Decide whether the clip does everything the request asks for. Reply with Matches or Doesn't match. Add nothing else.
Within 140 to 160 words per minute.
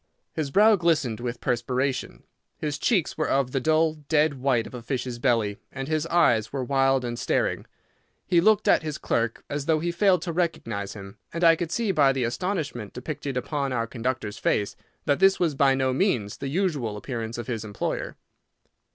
Doesn't match